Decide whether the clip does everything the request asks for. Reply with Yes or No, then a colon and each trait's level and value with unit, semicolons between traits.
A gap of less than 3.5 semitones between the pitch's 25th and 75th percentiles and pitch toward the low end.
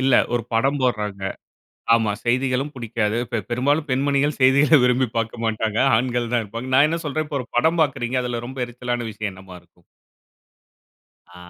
Yes: average, 3.1 semitones; low, 125 Hz